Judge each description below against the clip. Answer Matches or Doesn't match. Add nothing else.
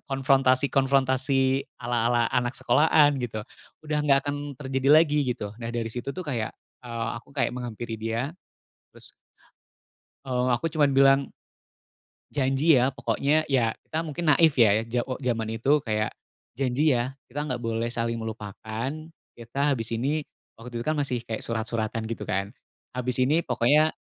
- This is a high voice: Doesn't match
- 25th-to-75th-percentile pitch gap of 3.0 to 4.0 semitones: Matches